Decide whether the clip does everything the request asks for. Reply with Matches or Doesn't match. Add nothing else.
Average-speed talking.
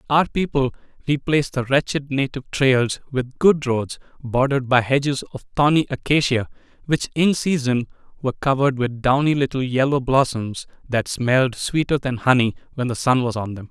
Matches